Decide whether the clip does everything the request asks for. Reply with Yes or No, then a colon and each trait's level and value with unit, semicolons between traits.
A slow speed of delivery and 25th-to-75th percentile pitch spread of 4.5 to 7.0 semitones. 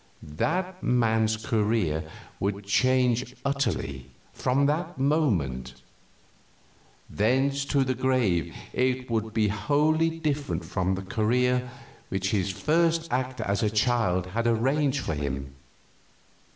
Yes: slow, 115 wpm; wide, 5.6 semitones